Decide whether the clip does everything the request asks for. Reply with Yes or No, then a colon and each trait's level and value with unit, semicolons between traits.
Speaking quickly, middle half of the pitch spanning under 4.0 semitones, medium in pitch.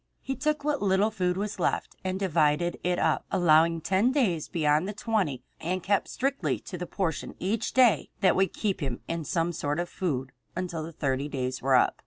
No: fast, 225 wpm; average, 4.5 semitones; medium, 180 Hz